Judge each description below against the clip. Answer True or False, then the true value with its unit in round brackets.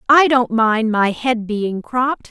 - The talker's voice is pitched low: False (235 Hz)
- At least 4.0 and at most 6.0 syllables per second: False (3.8 syllables/s)